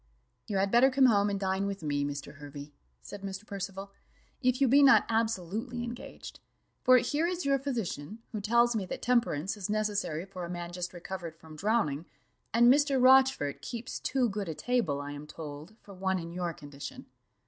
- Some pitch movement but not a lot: No, wide, 6.2 semitones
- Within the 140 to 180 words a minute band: No, average, 190 wpm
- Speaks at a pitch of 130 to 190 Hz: No, high, 200 Hz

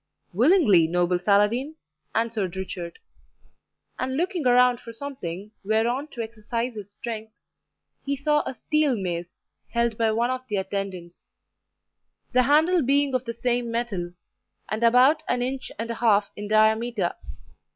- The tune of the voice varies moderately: Yes, average, 3.9 semitones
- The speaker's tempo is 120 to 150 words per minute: Yes, average, 140 wpm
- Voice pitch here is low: No, high, 230 Hz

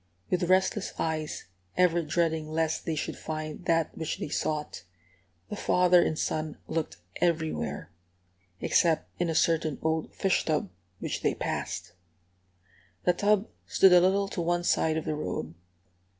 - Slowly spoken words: No, average, 150 wpm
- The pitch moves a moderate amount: No, narrow, 2.3 semitones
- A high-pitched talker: No, medium, 165 Hz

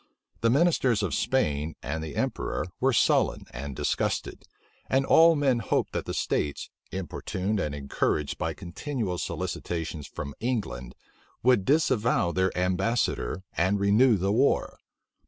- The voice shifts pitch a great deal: Yes, wide, 7.6 semitones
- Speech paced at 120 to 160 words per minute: Yes, slow, 135 wpm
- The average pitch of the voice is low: Yes, very low, 95 Hz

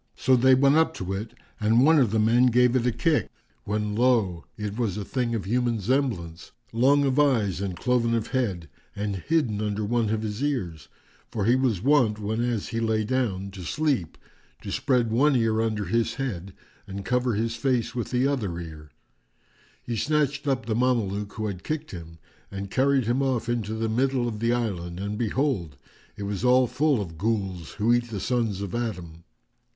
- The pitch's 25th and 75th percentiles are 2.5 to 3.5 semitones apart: No, average, 4.0 semitones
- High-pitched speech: No, low, 115 Hz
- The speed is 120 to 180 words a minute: No, average, 195 wpm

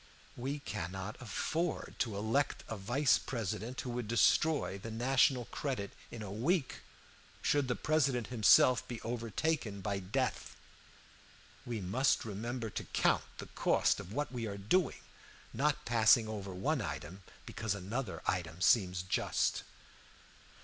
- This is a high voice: No, low, 115 Hz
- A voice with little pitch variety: No, average, 4.6 semitones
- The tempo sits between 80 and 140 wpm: Yes, slow, 135 wpm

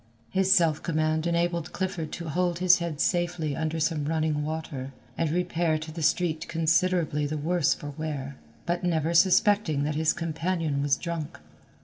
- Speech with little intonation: Yes, narrow, 2.1 semitones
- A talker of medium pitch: Yes, medium, 160 Hz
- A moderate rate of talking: Yes, average, 160 wpm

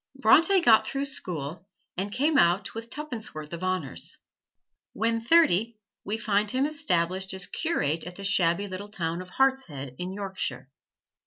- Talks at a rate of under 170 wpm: Yes, average, 155 wpm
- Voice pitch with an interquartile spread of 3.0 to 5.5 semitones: Yes, average, 5.2 semitones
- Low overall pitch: No, high, 200 Hz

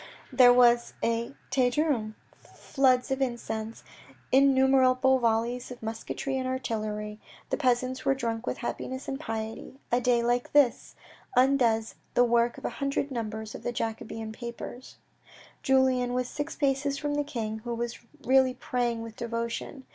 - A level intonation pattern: Yes, narrow, 2.3 semitones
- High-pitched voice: Yes, high, 245 Hz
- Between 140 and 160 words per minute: Yes, average, 155 wpm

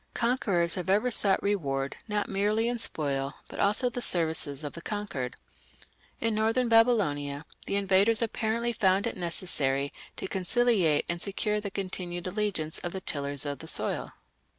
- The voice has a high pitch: Yes, high, 195 Hz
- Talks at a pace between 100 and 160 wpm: Yes, average, 155 wpm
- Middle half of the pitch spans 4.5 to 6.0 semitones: Yes, wide, 5.5 semitones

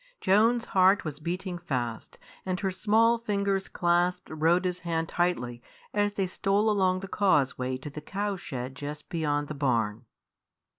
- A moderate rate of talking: Yes, average, 150 wpm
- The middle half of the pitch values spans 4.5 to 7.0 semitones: Yes, average, 5.0 semitones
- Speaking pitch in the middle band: Yes, medium, 175 Hz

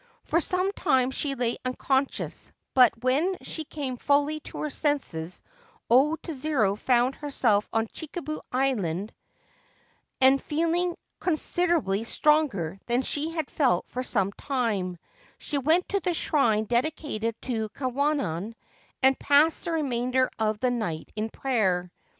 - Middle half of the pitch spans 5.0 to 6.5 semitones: Yes, wide, 5.4 semitones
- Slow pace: Yes, slow, 130 wpm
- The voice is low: No, very high, 265 Hz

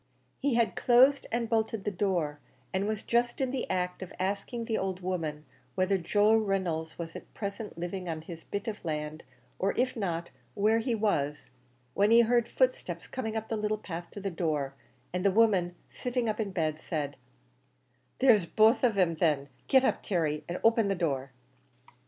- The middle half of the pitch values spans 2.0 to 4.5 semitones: No, average, 4.9 semitones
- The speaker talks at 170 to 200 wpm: Yes, average, 190 wpm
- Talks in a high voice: Yes, high, 195 Hz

